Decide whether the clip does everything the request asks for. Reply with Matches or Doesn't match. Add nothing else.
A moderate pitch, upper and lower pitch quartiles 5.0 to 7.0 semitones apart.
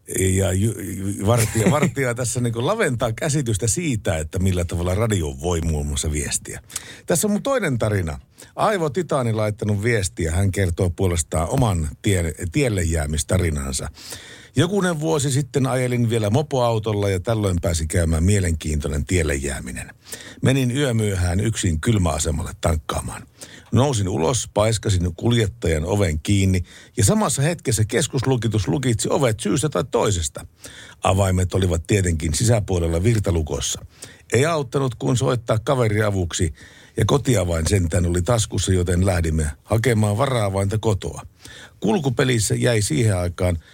Doesn't match